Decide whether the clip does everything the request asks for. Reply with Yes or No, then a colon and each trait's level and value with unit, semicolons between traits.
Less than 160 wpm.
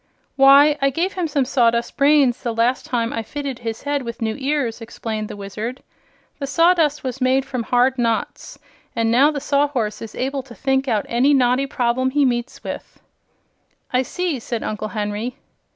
No: average, 180 wpm